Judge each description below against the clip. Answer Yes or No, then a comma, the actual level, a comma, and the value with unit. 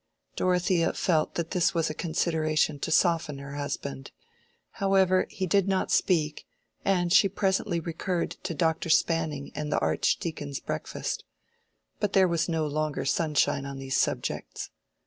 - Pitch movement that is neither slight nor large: Yes, average, 3.2 semitones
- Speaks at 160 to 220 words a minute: No, average, 145 wpm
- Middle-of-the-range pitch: Yes, medium, 165 Hz